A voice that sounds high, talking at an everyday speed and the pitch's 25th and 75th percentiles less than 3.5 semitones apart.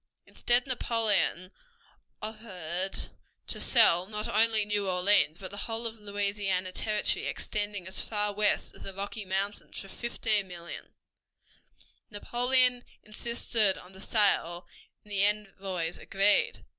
No: high, 205 Hz; slow, 120 wpm; narrow, 2.5 semitones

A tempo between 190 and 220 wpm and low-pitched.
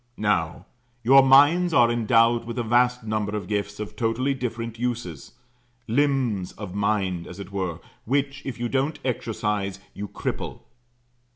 No: average, 150 wpm; low, 115 Hz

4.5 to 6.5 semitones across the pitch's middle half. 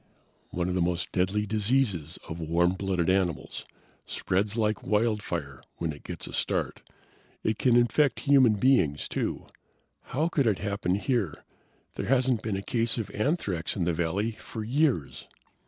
Yes: average, 5.2 semitones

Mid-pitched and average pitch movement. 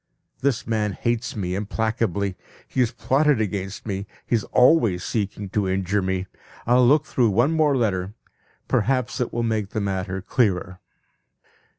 No: low, 110 Hz; average, 4.1 semitones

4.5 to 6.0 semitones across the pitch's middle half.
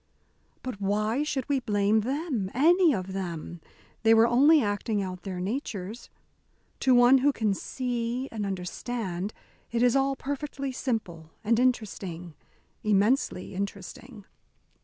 Yes: average, 4.8 semitones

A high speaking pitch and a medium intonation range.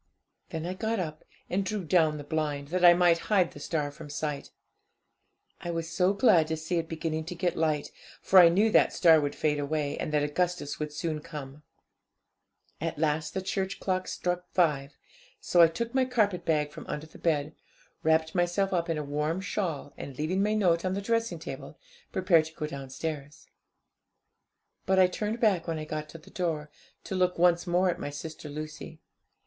No: medium, 165 Hz; average, 3.2 semitones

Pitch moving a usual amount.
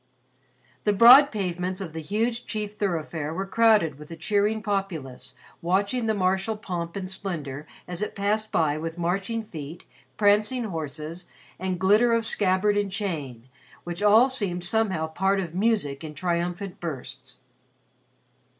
Yes: average, 4.2 semitones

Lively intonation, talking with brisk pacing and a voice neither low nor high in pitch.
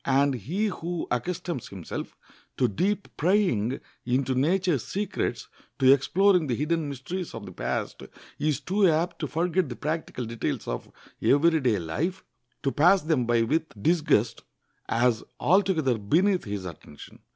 No: wide, 6.6 semitones; average, 145 wpm; medium, 150 Hz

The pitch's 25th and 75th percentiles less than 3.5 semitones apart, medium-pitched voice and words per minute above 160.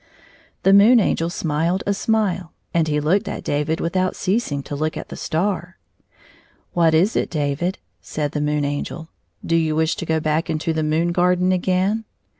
Yes: average, 3.1 semitones; medium, 165 Hz; average, 185 wpm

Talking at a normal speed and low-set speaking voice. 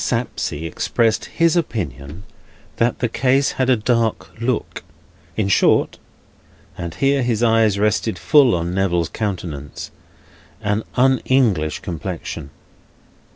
No: slow, 115 wpm; low, 110 Hz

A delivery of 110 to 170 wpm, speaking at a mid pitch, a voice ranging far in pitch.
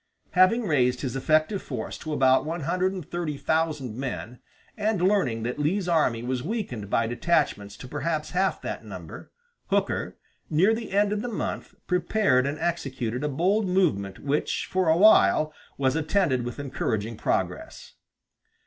Yes: average, 160 wpm; medium, 155 Hz; wide, 6.5 semitones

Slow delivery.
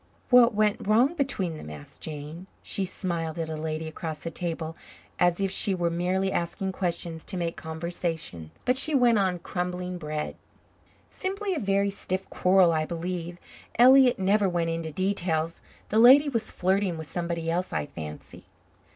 No: average, 165 wpm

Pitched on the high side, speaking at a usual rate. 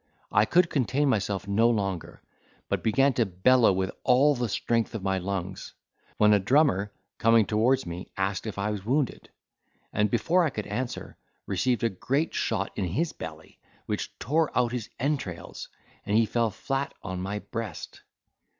No: low, 110 Hz; average, 170 wpm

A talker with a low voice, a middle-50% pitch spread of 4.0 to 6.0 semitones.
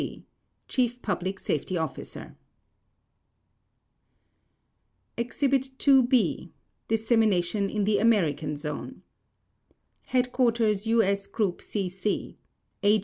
No: high, 210 Hz; average, 4.4 semitones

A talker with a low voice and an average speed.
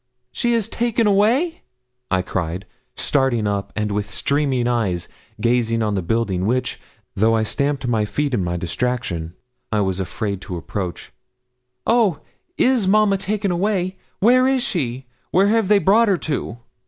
Yes: low, 125 Hz; average, 155 wpm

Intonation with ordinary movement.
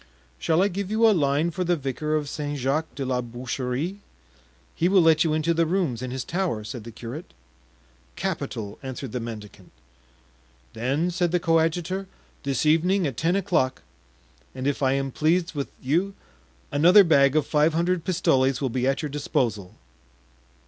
Yes: average, 4.8 semitones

